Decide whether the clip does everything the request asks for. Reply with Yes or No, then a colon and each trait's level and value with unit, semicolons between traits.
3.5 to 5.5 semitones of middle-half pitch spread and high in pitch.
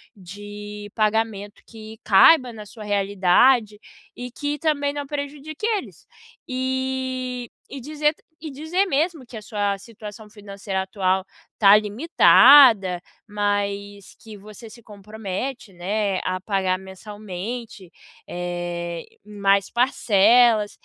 Yes: average, 4.4 semitones; high, 210 Hz